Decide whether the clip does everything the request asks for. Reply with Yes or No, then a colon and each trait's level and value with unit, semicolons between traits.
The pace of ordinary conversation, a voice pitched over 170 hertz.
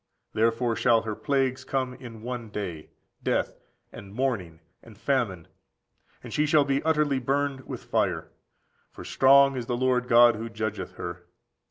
No: average, 155 wpm; low, 125 Hz